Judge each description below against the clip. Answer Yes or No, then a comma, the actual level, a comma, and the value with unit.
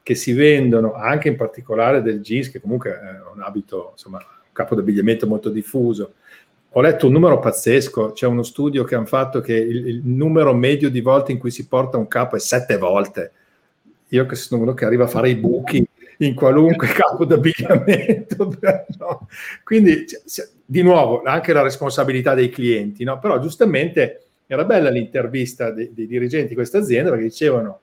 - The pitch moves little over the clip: No, average, 4.1 semitones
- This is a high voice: No, low, 130 Hz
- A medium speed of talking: No, fast, 175 wpm